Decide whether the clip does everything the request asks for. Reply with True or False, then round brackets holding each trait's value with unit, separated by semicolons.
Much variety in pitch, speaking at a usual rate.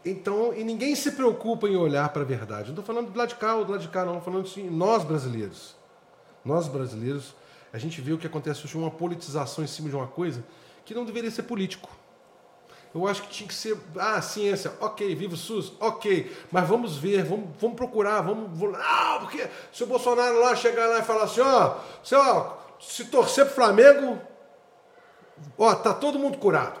False (6.2 semitones; 210 wpm)